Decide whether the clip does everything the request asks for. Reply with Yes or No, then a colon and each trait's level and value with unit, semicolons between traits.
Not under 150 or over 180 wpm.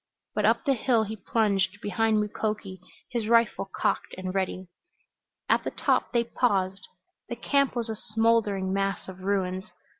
Yes: average, 155 wpm